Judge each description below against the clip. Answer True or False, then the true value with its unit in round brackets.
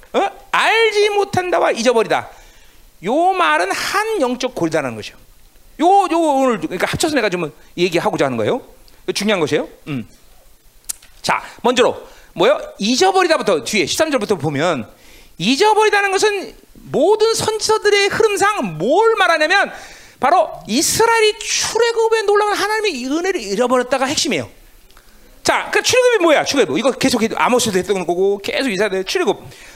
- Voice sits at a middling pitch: False (340 Hz)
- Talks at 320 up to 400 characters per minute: True (340 characters per minute)